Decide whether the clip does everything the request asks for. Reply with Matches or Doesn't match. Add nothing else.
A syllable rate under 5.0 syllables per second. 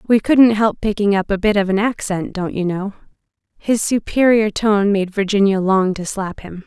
Matches